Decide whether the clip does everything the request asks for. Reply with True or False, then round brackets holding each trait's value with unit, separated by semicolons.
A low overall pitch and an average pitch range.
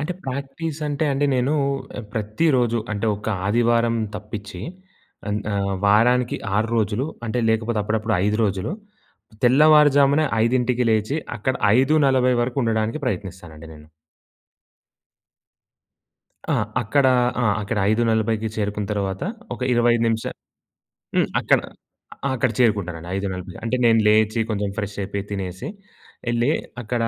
True (115 Hz; 3.4 semitones)